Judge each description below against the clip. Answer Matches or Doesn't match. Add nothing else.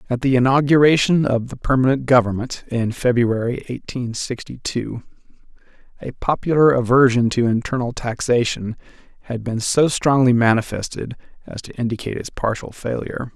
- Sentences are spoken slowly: Matches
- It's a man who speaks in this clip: Matches